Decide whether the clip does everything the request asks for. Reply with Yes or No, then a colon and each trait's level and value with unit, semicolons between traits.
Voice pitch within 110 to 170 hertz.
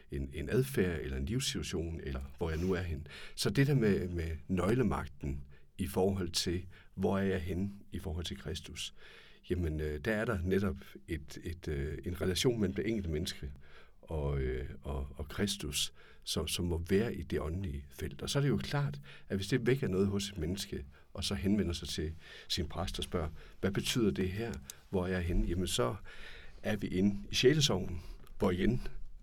No: very low, 90 Hz